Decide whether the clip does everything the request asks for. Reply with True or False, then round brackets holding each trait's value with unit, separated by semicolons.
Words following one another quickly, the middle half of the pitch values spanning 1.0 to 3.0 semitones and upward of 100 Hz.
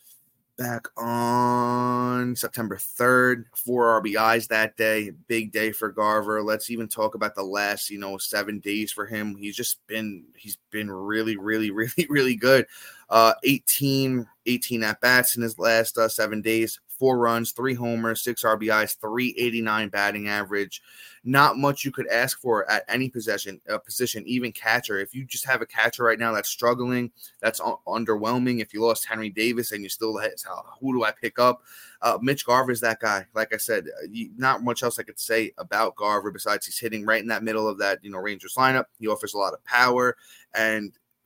False (195 wpm; 2.4 semitones; 115 Hz)